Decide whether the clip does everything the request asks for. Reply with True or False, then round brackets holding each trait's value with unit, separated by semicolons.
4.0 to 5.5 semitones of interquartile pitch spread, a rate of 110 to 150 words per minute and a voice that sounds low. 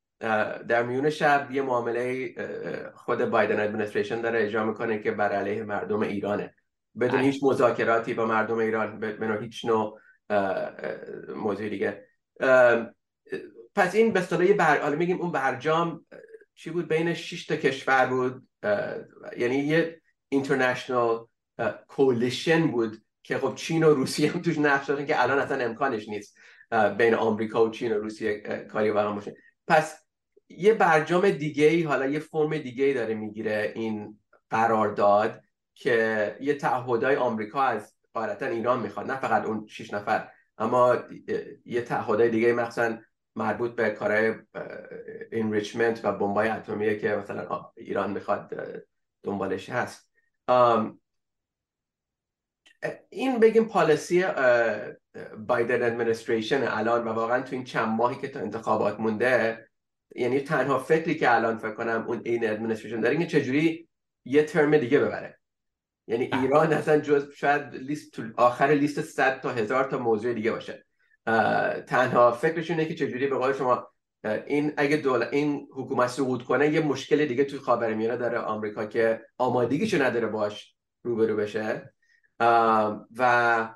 True (5.2 semitones; 140 wpm; 130 Hz)